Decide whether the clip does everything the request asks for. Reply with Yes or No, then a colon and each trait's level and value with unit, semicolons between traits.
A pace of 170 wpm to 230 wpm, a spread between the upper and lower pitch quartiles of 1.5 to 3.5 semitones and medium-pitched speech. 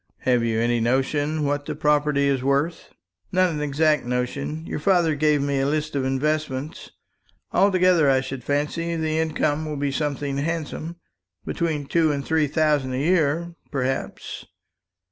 No: average, 155 wpm; narrow, 2.4 semitones; medium, 150 Hz